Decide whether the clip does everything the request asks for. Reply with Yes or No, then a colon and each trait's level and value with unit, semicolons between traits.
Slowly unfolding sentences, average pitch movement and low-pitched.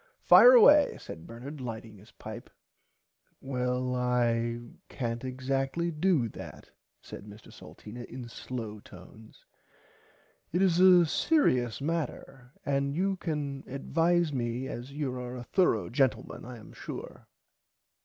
Yes: slow, 125 wpm; average, 4.5 semitones; low, 130 Hz